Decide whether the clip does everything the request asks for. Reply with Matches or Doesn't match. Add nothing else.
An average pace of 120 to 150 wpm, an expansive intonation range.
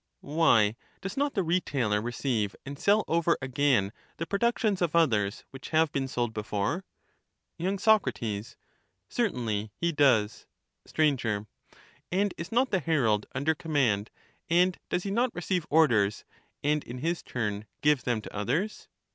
Matches